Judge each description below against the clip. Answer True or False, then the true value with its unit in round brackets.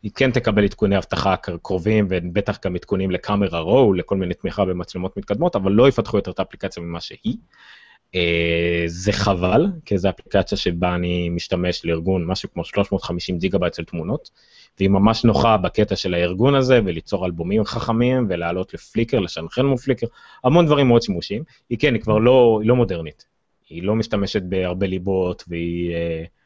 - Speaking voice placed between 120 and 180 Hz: False (95 Hz)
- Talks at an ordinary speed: False (170 wpm)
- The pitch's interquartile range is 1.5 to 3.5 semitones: False (4.1 semitones)